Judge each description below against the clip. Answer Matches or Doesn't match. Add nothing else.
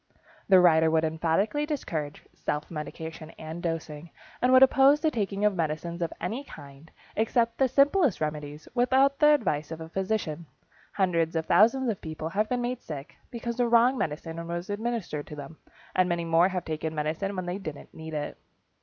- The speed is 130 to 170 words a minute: Doesn't match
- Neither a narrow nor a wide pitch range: Doesn't match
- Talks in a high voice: Doesn't match